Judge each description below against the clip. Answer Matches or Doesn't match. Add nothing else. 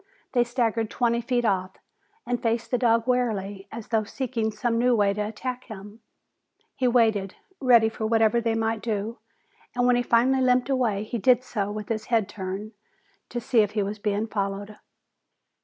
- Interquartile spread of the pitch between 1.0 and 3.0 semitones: Matches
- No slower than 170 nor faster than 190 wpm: Matches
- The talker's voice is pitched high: Matches